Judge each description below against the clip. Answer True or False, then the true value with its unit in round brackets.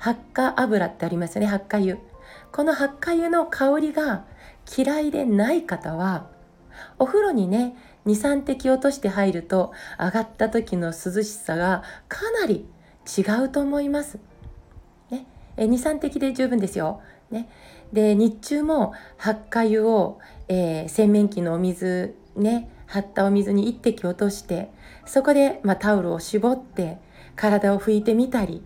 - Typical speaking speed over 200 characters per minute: True (260 characters per minute)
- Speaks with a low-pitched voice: False (215 Hz)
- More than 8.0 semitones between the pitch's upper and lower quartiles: False (5.2 semitones)